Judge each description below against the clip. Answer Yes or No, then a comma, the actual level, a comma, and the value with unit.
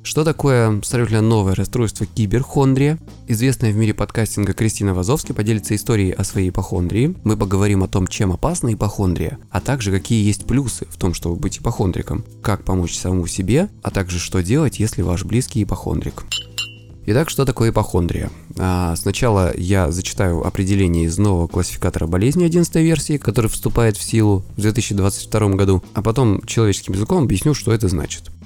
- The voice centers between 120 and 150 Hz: No, low, 105 Hz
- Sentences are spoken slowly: No, fast, 160 wpm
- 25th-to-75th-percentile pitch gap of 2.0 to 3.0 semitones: No, average, 3.7 semitones